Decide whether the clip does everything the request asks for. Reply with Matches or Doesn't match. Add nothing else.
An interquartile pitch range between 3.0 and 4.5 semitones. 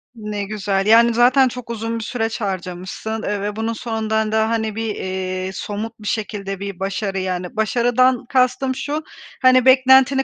Matches